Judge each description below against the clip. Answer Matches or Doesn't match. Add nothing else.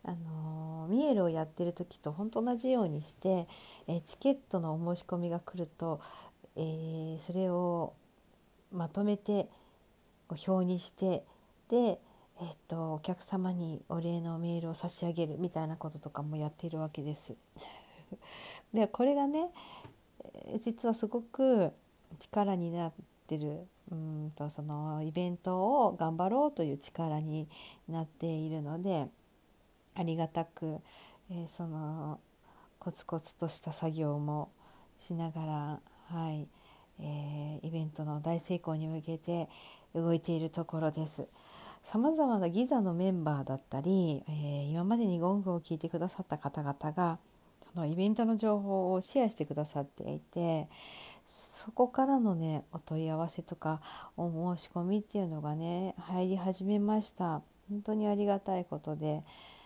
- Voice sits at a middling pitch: Matches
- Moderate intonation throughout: Matches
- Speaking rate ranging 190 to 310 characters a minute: Matches